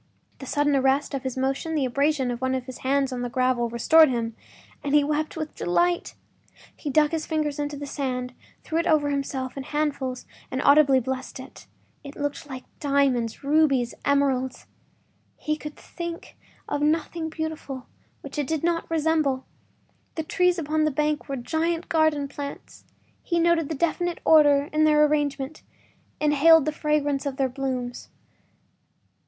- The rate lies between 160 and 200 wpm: Yes, average, 165 wpm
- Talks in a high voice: Yes, very high, 290 Hz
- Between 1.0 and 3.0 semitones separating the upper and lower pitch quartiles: Yes, average, 2.7 semitones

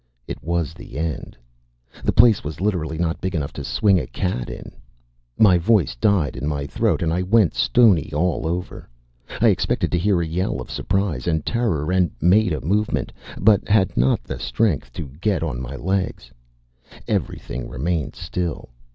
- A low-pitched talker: Yes, very low, 85 Hz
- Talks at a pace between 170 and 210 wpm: Yes, average, 175 wpm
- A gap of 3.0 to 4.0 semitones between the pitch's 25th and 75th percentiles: No, average, 4.4 semitones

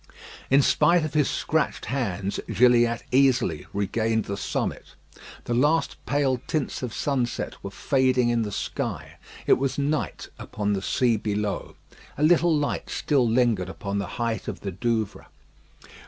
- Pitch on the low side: Yes, low, 120 Hz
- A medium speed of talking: Yes, average, 150 wpm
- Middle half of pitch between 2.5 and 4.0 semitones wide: No, average, 4.7 semitones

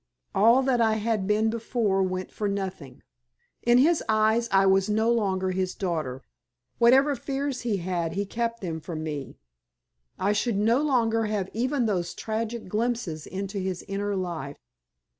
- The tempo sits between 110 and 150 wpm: No, average, 160 wpm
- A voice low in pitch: No, high, 210 Hz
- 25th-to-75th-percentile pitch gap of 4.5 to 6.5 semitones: No, average, 3.7 semitones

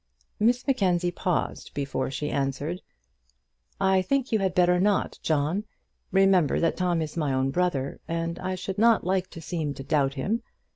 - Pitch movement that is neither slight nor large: Yes, average, 4.4 semitones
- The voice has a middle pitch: Yes, medium, 175 Hz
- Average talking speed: Yes, average, 165 wpm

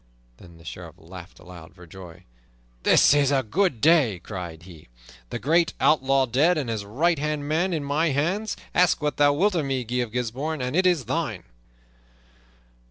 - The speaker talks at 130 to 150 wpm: No, average, 180 wpm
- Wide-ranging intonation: Yes, wide, 8.4 semitones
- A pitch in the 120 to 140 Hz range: Yes, low, 135 Hz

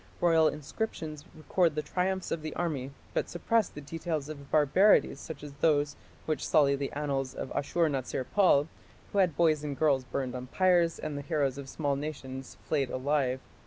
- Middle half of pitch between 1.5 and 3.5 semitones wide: Yes, average, 2.9 semitones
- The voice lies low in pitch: No, medium, 150 Hz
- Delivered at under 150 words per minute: No, average, 180 wpm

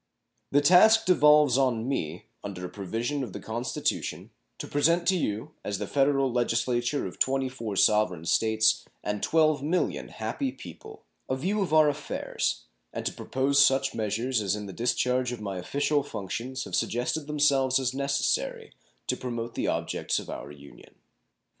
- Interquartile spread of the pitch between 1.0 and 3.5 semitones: No, average, 4.8 semitones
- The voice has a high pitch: No, low, 130 Hz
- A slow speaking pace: No, average, 160 wpm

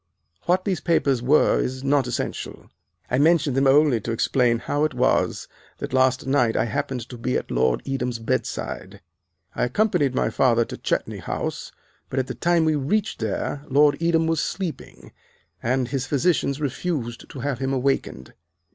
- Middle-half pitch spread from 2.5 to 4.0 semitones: Yes, average, 3.5 semitones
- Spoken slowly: No, average, 175 wpm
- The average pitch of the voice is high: No, low, 135 Hz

